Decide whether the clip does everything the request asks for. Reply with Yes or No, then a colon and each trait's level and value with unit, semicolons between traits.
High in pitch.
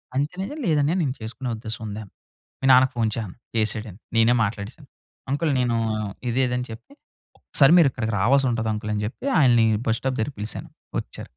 No: low, 120 Hz